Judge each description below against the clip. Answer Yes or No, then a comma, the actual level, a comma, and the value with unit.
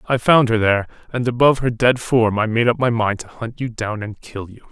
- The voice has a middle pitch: No, low, 115 Hz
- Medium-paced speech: No, fast, 265 wpm